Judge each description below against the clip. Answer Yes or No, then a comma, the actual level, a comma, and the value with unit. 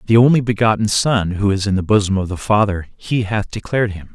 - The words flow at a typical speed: No, fast, 230 wpm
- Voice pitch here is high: No, low, 105 Hz